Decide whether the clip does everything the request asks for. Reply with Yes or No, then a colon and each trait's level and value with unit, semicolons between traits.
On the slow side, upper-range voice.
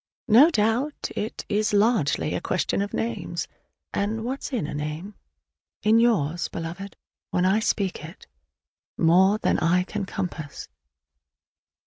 Yes: slow, 130 wpm; high, 200 Hz